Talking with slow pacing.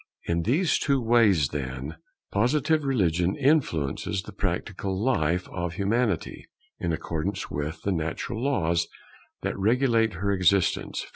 Yes: slow, 125 wpm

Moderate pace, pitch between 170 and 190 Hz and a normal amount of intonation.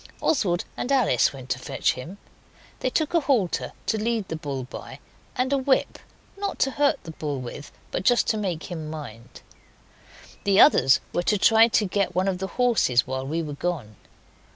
No: average, 190 wpm; medium, 185 Hz; wide, 8.4 semitones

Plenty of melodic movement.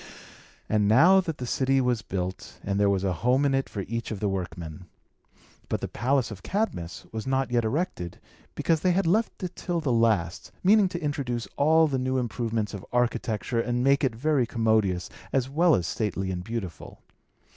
Yes: wide, 5.8 semitones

